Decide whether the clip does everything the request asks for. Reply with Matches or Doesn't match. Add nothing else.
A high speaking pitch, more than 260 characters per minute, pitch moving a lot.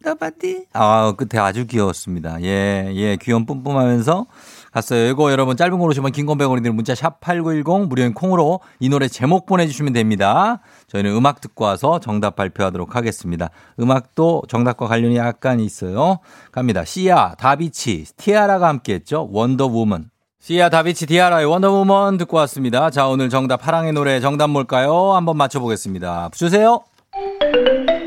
Doesn't match